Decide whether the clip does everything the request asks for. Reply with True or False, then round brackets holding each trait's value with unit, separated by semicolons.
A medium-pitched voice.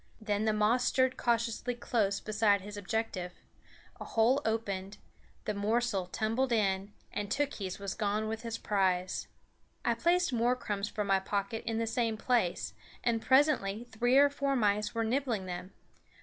False (220 Hz)